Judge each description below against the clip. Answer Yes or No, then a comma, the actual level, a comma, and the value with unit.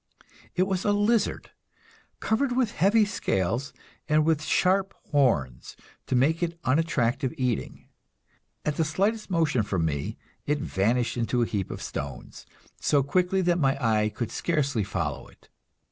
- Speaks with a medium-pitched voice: Yes, medium, 150 Hz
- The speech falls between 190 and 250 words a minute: No, average, 145 wpm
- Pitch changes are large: Yes, wide, 7.5 semitones